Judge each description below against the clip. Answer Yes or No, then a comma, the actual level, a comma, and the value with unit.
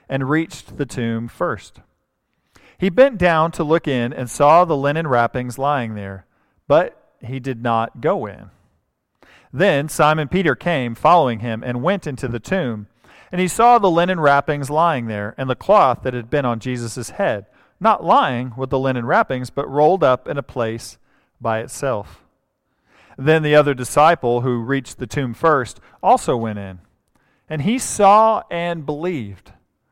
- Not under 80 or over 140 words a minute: No, average, 165 wpm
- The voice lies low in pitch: Yes, low, 130 Hz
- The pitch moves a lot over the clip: No, average, 4.9 semitones